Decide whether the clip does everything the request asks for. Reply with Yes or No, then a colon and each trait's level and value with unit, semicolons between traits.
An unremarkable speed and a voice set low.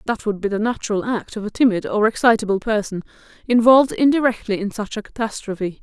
No: average, 185 wpm; high, 220 Hz